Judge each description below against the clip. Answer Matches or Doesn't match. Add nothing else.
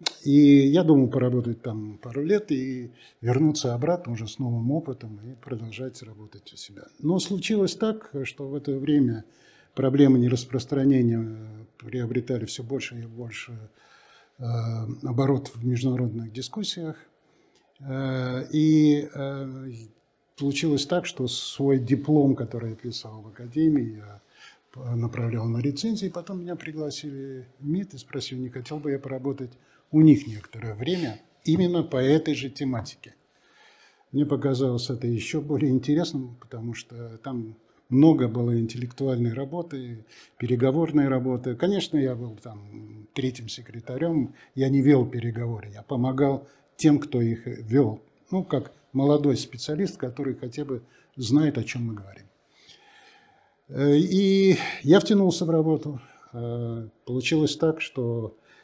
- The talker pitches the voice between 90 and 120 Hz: Doesn't match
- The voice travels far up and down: Doesn't match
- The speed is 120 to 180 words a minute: Matches